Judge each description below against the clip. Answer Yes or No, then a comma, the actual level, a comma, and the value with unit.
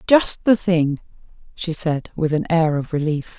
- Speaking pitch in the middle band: Yes, medium, 165 Hz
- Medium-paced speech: Yes, average, 175 wpm